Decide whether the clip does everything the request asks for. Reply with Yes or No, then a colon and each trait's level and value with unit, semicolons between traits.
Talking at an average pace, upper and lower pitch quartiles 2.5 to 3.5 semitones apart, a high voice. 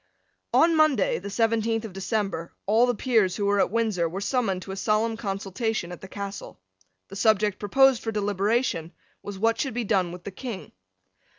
Yes: average, 185 wpm; average, 2.9 semitones; high, 210 Hz